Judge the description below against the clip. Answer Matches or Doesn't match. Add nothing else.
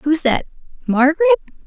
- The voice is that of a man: Doesn't match